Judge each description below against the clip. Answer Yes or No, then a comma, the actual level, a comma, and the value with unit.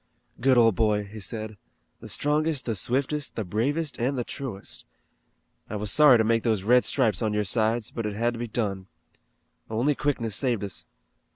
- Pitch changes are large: No, average, 3.6 semitones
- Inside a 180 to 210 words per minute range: Yes, average, 185 wpm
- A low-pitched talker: Yes, low, 115 Hz